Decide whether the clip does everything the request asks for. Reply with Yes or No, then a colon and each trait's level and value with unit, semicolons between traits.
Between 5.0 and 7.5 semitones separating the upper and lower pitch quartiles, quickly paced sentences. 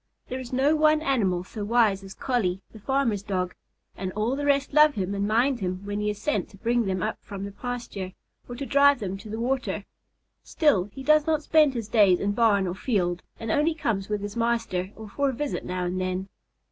Yes: wide, 5.4 semitones; fast, 225 wpm